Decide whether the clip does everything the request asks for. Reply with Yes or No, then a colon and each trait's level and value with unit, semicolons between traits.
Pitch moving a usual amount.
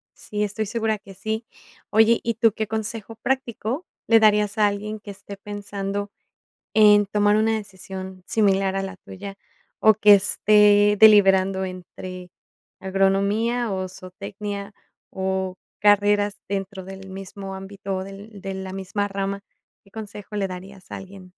No: narrow, 1.6 semitones